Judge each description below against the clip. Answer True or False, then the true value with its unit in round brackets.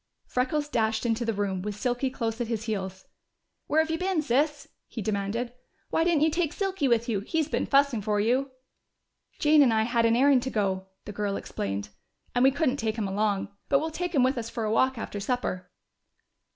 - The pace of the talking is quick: True (210 wpm)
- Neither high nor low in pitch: False (240 Hz)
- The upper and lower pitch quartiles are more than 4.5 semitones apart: True (5.0 semitones)